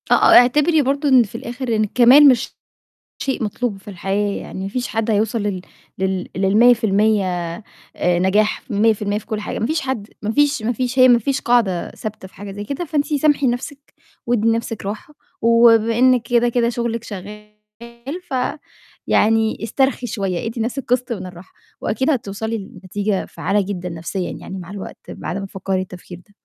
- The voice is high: Yes, high, 225 Hz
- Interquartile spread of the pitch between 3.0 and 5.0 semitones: Yes, average, 3.7 semitones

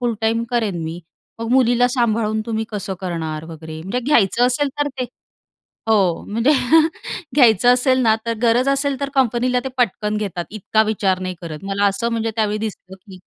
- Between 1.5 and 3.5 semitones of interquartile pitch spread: No, average, 4.1 semitones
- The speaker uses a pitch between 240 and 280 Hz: No, high, 220 Hz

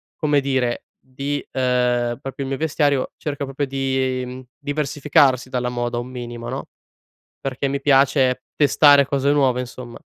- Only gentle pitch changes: Yes, narrow, 2.1 semitones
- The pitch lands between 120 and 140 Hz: Yes, low, 135 Hz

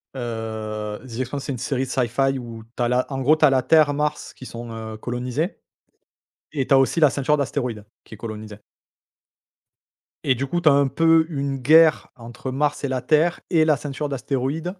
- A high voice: No, low, 135 Hz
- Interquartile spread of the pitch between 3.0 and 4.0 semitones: Yes, average, 3.7 semitones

